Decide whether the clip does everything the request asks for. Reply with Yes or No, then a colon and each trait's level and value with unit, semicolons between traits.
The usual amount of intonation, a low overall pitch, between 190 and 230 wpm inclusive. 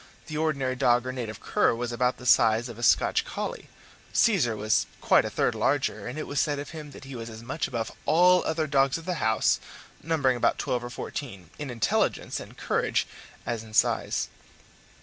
Yes: average, 4.0 semitones; low, 125 Hz; average, 200 wpm